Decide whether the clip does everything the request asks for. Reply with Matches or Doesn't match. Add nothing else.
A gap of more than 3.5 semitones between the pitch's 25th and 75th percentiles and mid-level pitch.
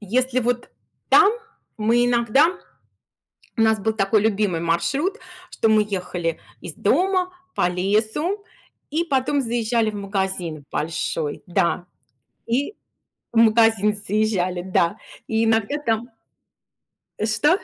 Doesn't match